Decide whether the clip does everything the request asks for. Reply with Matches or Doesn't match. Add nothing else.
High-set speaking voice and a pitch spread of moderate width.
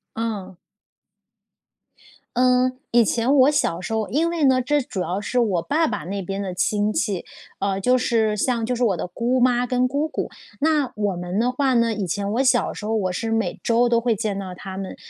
Matches